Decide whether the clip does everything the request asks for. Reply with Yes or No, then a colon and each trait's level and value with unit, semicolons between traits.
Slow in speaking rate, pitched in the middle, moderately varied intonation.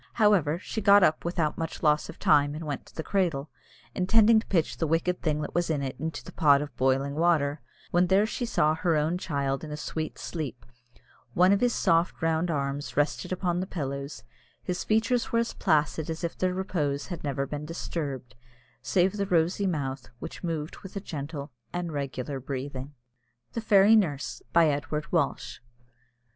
No: average, 185 wpm; medium, 160 Hz; average, 4.0 semitones